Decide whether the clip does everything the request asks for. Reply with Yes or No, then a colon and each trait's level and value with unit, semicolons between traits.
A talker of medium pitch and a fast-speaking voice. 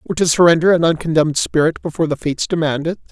Yes: medium, 160 Hz; fast, 210 wpm